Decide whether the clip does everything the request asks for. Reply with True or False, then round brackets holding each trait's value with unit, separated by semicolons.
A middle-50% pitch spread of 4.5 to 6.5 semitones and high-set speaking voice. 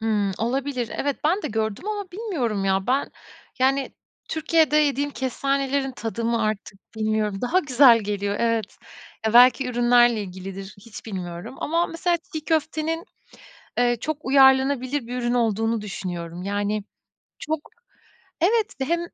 True (5.0 semitones; 245 Hz)